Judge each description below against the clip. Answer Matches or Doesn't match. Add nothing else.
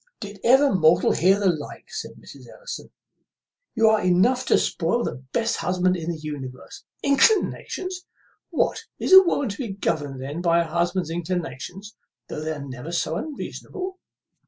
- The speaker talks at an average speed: Matches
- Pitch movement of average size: Doesn't match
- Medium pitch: Matches